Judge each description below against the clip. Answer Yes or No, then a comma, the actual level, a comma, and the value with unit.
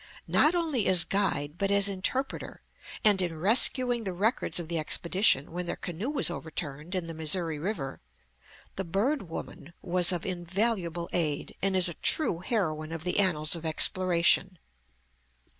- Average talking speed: Yes, average, 160 wpm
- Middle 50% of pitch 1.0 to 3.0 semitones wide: No, average, 3.4 semitones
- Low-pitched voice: No, medium, 180 Hz